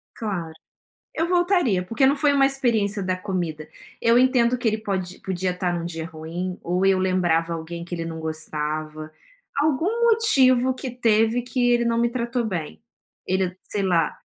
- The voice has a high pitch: Yes, high, 195 Hz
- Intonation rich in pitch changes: Yes, wide, 6.4 semitones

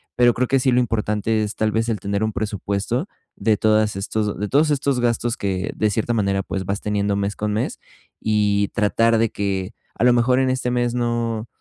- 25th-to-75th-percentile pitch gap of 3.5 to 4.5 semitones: No, average, 2.8 semitones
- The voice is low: Yes, low, 110 Hz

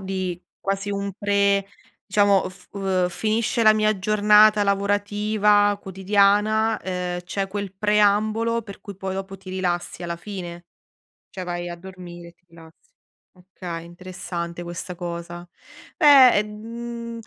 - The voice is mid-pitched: No, high, 195 Hz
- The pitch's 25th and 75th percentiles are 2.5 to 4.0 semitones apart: Yes, average, 2.8 semitones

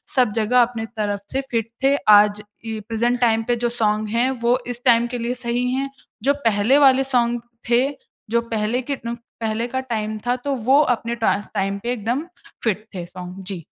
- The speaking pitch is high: Yes, high, 235 Hz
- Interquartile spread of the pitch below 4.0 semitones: Yes, narrow, 2.4 semitones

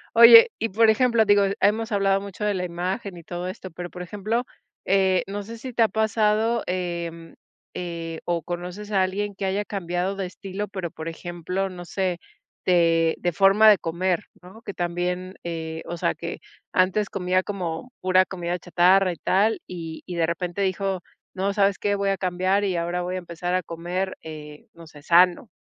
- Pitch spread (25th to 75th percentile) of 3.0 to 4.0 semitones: No, narrow, 2.5 semitones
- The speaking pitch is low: No, medium, 185 Hz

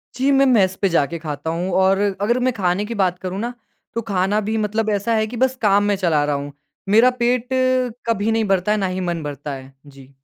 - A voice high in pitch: Yes, high, 195 Hz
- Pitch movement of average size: Yes, average, 4.7 semitones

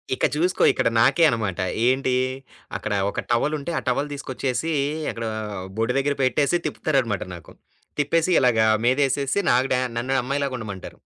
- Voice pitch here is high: No, low, 130 Hz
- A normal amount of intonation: Yes, average, 3.4 semitones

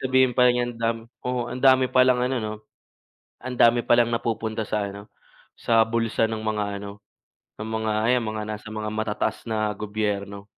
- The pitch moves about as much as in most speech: No, narrow, 2.2 semitones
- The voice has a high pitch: No, low, 110 Hz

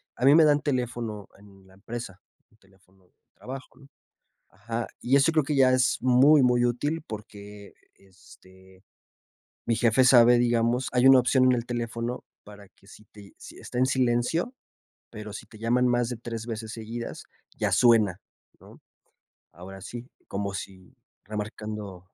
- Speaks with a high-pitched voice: No, low, 115 Hz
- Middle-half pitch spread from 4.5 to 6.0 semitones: No, average, 3.6 semitones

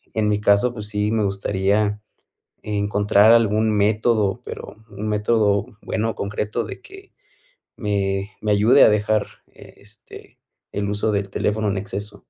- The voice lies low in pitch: Yes, low, 105 Hz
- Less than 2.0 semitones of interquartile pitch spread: Yes, narrow, 1.2 semitones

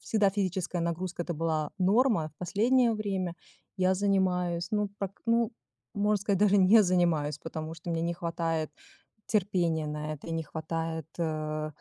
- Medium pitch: Yes, medium, 175 Hz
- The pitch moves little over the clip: No, average, 3.6 semitones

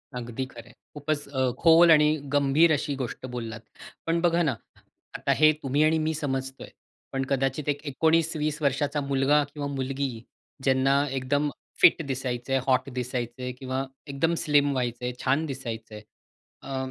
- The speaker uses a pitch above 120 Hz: Yes, low, 135 Hz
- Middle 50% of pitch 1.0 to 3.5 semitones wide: Yes, narrow, 2.5 semitones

